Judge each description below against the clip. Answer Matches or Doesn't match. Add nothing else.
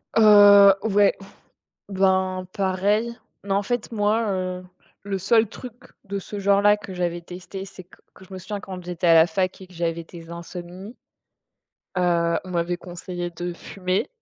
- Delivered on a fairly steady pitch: Matches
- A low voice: Doesn't match